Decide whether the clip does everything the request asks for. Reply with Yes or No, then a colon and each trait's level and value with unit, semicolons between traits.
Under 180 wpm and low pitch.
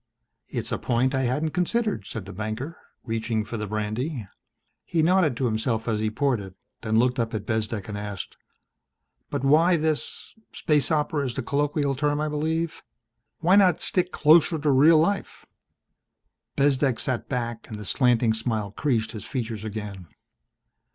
Yes: average, 165 wpm; low, 125 Hz